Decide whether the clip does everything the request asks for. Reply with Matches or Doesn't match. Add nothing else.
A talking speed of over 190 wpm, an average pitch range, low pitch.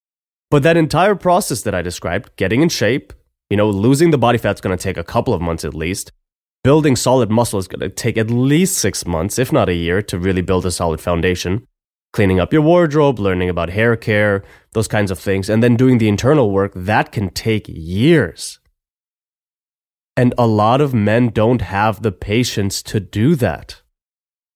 Matches